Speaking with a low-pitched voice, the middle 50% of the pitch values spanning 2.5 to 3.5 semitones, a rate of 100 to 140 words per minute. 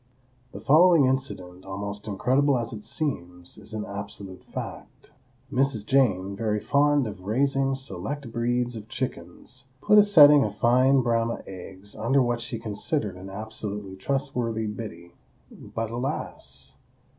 No: low, 115 Hz; average, 4.9 semitones; slow, 135 wpm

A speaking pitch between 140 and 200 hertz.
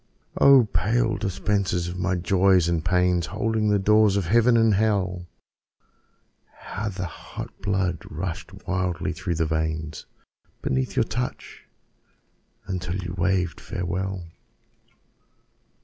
No: very low, 95 Hz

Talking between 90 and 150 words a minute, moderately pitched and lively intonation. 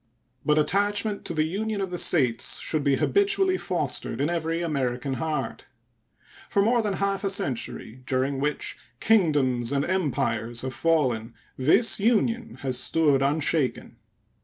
Yes: average, 140 wpm; medium, 155 Hz; wide, 7.0 semitones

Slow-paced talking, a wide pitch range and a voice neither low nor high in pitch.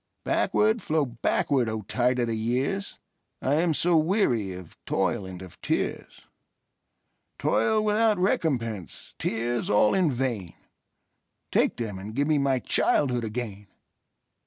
No: slow, 120 wpm; wide, 6.4 semitones; low, 125 Hz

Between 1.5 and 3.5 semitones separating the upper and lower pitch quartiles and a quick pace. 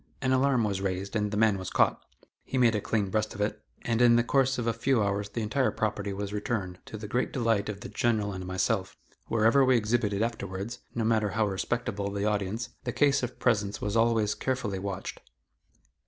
Yes: average, 2.8 semitones; fast, 210 wpm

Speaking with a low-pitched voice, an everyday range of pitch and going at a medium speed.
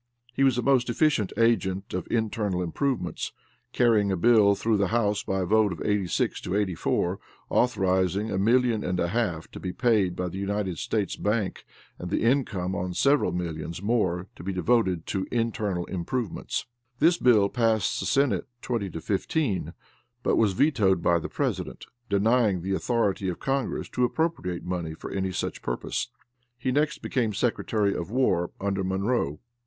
Yes: low, 100 Hz; average, 4.4 semitones; average, 170 wpm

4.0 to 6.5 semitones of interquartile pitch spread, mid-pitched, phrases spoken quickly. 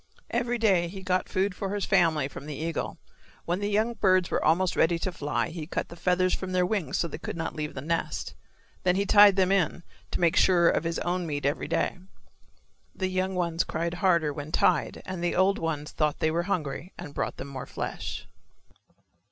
No: average, 2.8 semitones; medium, 175 Hz; fast, 210 wpm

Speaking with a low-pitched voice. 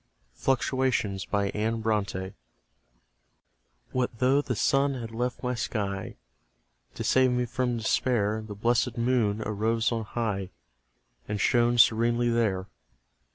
Yes: low, 115 Hz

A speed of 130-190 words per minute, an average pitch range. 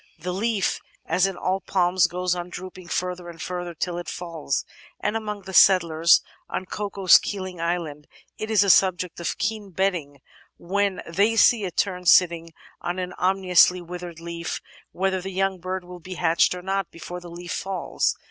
No: average, 175 wpm; narrow, 1.9 semitones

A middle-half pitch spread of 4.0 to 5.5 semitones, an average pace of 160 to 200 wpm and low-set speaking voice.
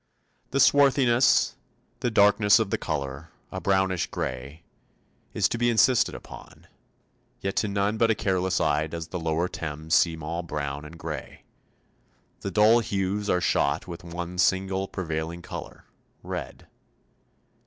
No: average, 4.3 semitones; average, 145 wpm; very low, 90 Hz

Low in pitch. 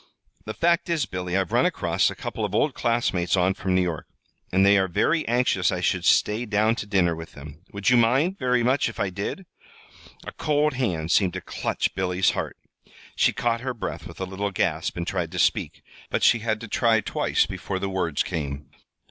Yes: low, 100 Hz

